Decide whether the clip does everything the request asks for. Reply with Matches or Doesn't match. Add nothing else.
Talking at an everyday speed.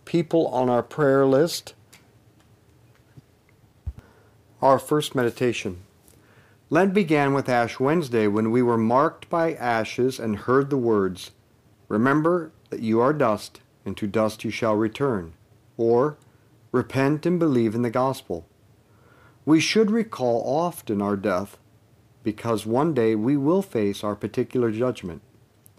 Doesn't match